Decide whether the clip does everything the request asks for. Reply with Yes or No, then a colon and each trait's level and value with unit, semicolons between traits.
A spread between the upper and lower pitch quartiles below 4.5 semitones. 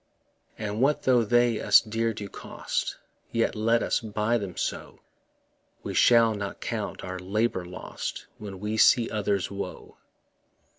Yes: narrow, 2.4 semitones